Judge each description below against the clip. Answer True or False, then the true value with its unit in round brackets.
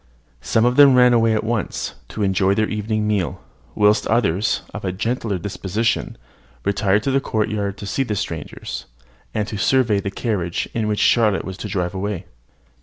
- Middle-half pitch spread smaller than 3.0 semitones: True (2.5 semitones)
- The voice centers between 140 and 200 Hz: False (105 Hz)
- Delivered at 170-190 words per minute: True (180 wpm)